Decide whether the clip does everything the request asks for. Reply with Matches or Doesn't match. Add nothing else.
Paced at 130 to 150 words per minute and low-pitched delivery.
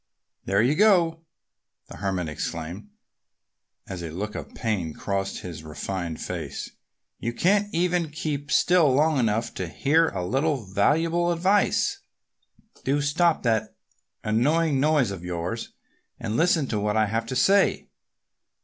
Matches